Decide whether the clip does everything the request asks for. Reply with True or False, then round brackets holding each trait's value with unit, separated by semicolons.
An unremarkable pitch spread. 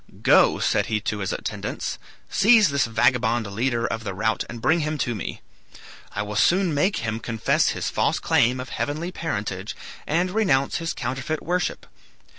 False (6.5 semitones)